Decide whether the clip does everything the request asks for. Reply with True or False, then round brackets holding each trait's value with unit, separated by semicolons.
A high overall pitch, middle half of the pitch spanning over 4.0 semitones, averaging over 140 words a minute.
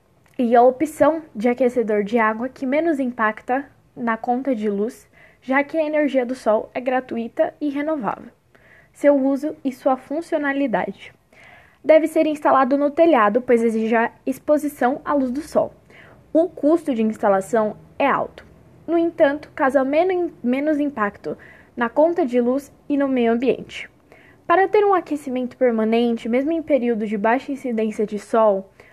True (265 Hz; 4.4 semitones; 155 wpm)